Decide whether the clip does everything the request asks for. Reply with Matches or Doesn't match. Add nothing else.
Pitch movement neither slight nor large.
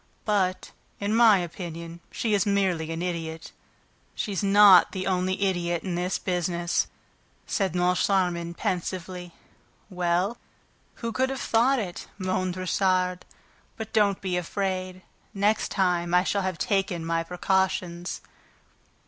Doesn't match